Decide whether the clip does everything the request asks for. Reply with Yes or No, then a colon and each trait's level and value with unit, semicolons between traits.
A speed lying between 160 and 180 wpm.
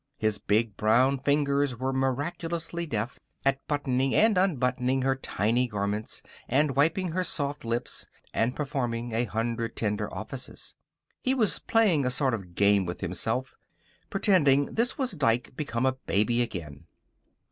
No: average, 145 wpm